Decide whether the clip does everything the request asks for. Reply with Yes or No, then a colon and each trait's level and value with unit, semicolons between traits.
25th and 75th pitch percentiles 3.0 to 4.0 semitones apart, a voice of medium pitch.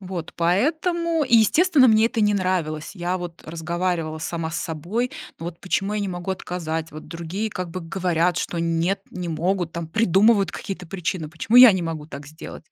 Yes: average, 3.6 semitones; medium, 180 Hz